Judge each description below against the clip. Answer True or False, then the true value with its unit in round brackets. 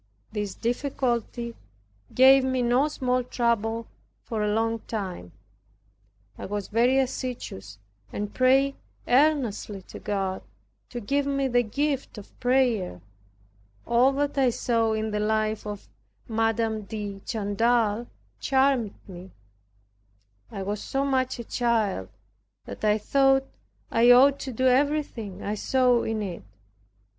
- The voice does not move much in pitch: False (3.8 semitones)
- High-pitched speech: True (235 Hz)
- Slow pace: True (130 wpm)